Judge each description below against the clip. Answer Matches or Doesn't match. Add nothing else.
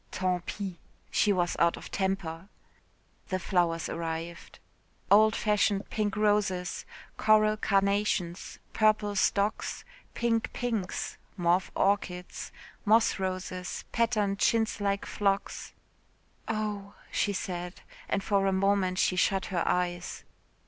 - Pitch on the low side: Doesn't match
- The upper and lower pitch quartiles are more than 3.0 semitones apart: Doesn't match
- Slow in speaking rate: Matches